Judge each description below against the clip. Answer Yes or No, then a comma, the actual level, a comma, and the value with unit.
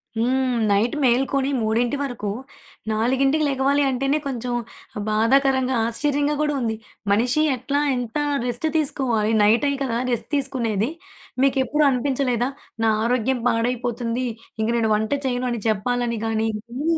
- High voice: Yes, very high, 250 Hz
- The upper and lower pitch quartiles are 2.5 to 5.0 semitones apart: Yes, average, 3.0 semitones